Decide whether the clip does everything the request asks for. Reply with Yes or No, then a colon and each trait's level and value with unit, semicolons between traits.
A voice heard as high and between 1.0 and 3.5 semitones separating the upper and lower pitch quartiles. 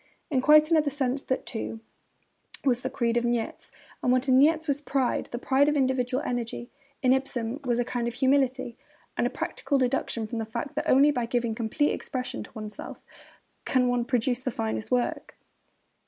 Yes: very high, 255 Hz; narrow, 2.5 semitones